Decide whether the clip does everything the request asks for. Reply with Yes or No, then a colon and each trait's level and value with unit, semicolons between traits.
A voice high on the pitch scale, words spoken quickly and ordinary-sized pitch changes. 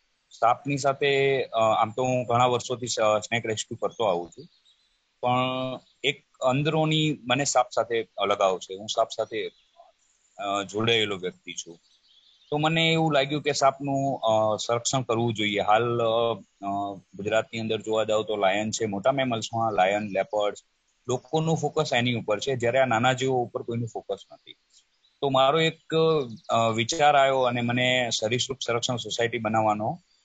No: low, 120 Hz; fast, 145 wpm; average, 3.8 semitones